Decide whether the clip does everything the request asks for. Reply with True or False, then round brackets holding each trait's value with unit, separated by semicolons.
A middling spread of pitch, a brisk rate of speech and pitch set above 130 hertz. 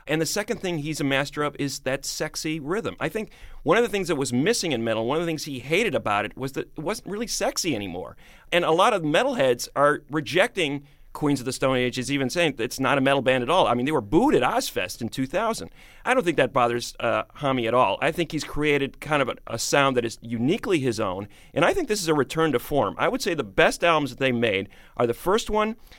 True (4.0 semitones; 260 wpm; 140 Hz)